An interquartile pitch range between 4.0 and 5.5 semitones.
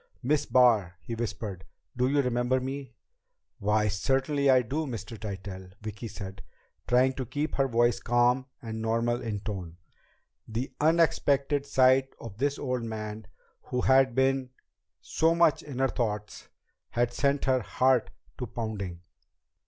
No: average, 3.6 semitones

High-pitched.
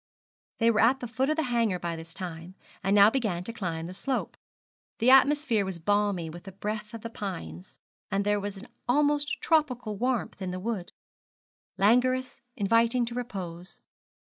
Yes: high, 210 Hz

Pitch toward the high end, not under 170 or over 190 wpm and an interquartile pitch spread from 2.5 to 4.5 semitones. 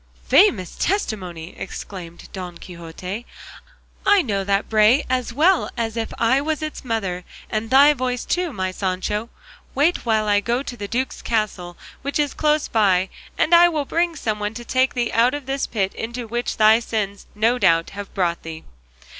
No: high, 225 Hz; average, 180 wpm; average, 5.2 semitones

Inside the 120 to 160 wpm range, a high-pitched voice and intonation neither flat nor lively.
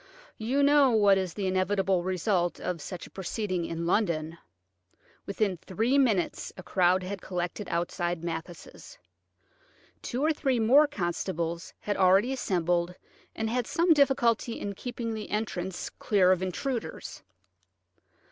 Yes: slow, 135 wpm; high, 195 Hz; average, 4.7 semitones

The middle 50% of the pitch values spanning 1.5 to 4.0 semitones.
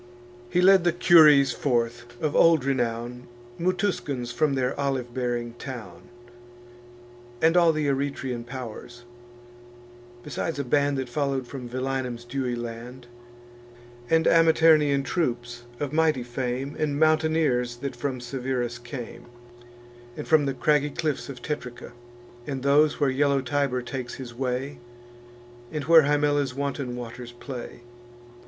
Yes: average, 3.2 semitones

